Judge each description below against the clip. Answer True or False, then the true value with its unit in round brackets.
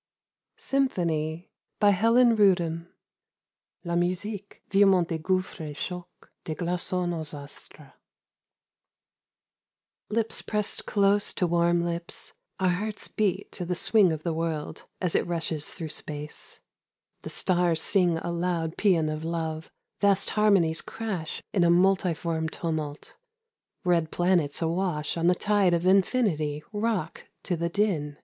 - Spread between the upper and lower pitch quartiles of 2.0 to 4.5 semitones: True (3.2 semitones)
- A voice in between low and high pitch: True (175 Hz)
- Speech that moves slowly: True (130 wpm)